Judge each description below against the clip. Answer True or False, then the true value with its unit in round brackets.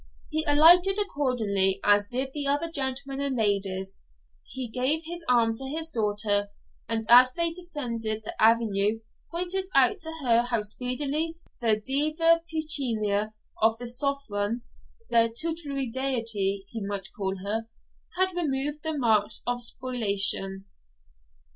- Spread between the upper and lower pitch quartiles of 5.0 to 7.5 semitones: True (5.4 semitones)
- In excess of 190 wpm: False (135 wpm)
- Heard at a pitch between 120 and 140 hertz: False (245 Hz)